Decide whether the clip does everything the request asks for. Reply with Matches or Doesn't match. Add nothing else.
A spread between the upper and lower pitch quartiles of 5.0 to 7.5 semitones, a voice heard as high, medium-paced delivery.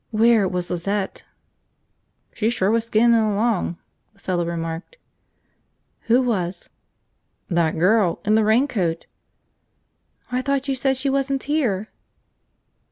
Doesn't match